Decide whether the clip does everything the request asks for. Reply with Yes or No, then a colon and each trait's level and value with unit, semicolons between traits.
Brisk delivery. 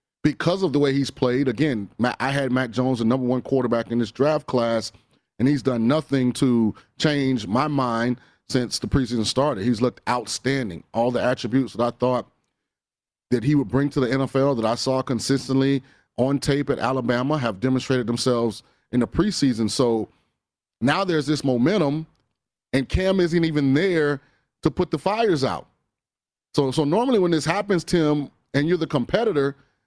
No: average, 175 wpm